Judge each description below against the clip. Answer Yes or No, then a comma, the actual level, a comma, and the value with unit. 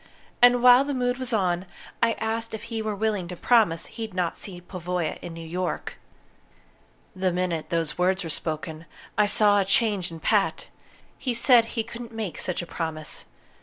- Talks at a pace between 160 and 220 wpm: Yes, average, 180 wpm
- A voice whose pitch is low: No, high, 195 Hz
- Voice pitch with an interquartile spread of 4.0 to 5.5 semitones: Yes, average, 4.7 semitones